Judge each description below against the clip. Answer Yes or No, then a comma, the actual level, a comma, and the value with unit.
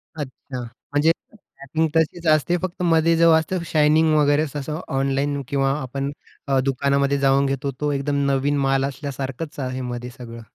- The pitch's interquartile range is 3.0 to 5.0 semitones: No, narrow, 2.4 semitones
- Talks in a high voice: No, medium, 140 Hz